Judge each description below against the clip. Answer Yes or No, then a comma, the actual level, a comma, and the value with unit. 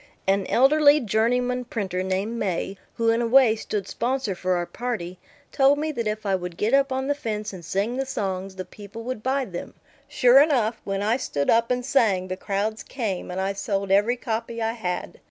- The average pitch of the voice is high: Yes, high, 220 Hz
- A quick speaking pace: Yes, fast, 210 wpm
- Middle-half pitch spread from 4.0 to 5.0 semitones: Yes, average, 4.4 semitones